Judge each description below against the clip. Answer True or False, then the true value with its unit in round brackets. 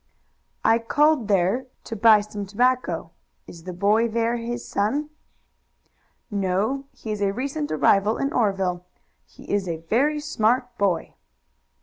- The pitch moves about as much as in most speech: True (4.2 semitones)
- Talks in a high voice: True (220 Hz)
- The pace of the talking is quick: False (135 wpm)